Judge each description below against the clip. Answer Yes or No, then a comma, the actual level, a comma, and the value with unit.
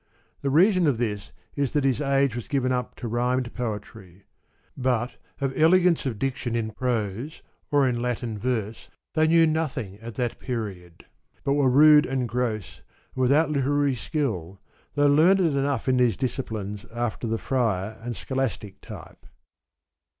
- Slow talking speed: No, average, 155 wpm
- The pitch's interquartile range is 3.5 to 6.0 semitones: Yes, average, 3.9 semitones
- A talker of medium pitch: No, low, 125 Hz